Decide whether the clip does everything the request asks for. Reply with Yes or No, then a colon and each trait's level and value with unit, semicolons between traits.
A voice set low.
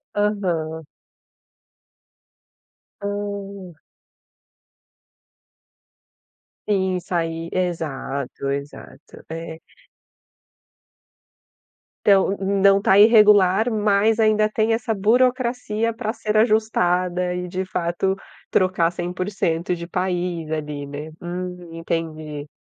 No: medium, 185 Hz